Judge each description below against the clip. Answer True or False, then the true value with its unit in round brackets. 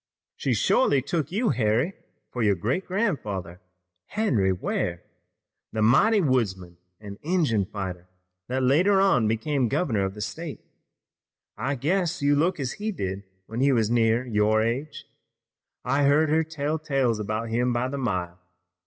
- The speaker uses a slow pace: False (155 wpm)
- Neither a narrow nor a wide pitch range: False (6.4 semitones)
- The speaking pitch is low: True (125 Hz)